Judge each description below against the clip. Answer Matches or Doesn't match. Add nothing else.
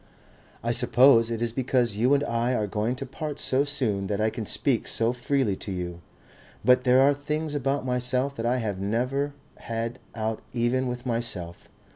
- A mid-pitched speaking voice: Doesn't match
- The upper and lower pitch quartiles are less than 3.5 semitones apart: Matches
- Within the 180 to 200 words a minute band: Matches